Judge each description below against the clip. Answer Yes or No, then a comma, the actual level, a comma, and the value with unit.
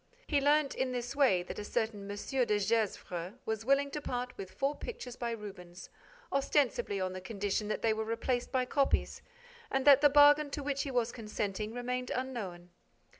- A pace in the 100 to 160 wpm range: No, average, 185 wpm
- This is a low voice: No, high, 240 Hz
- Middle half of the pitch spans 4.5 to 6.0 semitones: Yes, average, 4.8 semitones